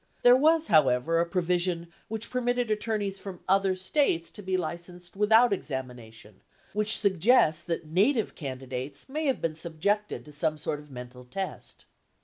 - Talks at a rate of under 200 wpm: Yes, average, 155 wpm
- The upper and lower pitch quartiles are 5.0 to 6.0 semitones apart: Yes, wide, 5.6 semitones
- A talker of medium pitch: Yes, medium, 180 Hz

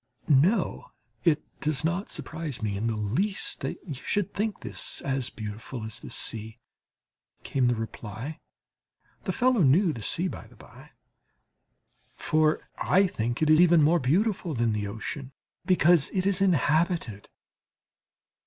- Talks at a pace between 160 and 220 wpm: No, average, 145 wpm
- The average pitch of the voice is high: No, medium, 150 Hz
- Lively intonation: Yes, wide, 7.4 semitones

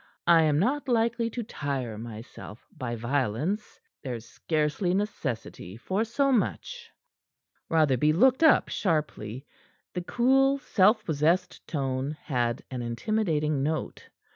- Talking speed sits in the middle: No, slow, 115 wpm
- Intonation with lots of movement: Yes, wide, 8.9 semitones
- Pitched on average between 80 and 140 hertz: No, medium, 155 Hz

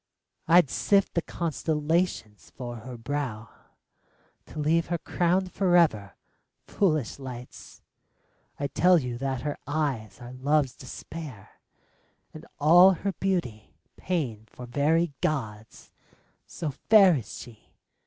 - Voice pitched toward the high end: No, medium, 145 Hz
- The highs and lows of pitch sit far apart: Yes, wide, 5.8 semitones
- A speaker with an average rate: No, slow, 115 wpm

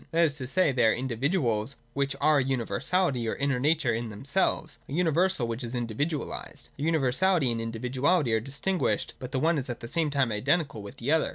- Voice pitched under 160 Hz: Yes, low, 135 Hz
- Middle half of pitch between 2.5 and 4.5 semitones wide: No, average, 4.9 semitones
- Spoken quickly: Yes, fast, 210 wpm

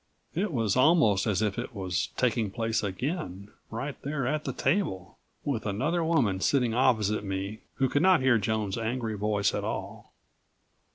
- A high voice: No, low, 115 Hz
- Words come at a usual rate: Yes, average, 165 wpm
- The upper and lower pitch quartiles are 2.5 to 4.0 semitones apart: No, average, 5.2 semitones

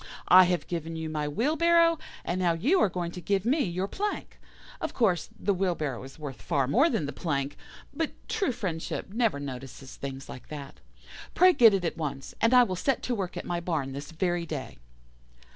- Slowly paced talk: No, average, 200 wpm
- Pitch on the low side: No, medium, 175 Hz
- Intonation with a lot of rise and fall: Yes, wide, 7.6 semitones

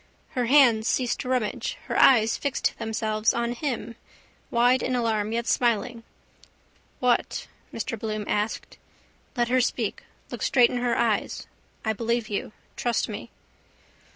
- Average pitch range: No, narrow, 2.1 semitones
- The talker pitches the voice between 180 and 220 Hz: No, high, 235 Hz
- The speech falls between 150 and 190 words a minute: No, average, 140 wpm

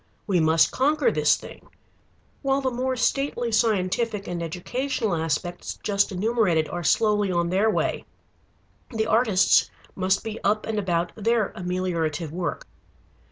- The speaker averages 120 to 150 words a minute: Yes, slow, 135 wpm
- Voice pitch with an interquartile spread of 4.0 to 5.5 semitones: Yes, average, 4.7 semitones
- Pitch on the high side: Yes, high, 200 Hz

